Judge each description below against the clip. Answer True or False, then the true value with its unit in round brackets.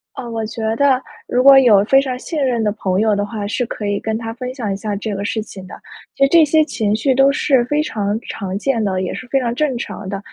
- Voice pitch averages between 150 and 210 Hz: False (230 Hz)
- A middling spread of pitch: True (4.5 semitones)